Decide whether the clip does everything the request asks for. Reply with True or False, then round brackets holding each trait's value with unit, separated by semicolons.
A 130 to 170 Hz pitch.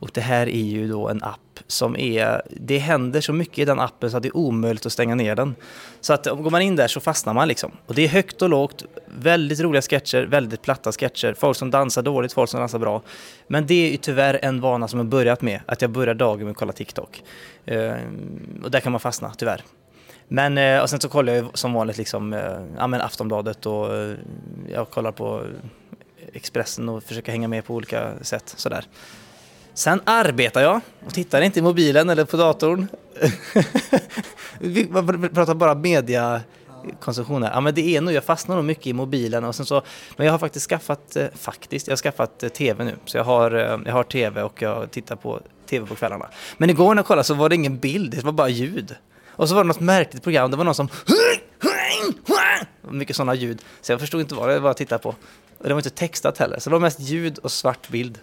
True (140 Hz)